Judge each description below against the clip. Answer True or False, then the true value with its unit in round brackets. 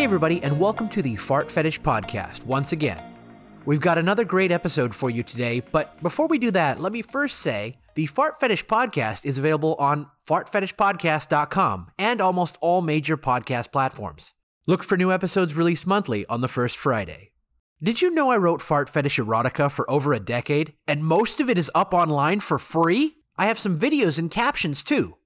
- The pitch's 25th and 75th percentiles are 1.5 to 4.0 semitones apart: False (5.5 semitones)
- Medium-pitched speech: True (160 Hz)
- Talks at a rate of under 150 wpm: False (190 wpm)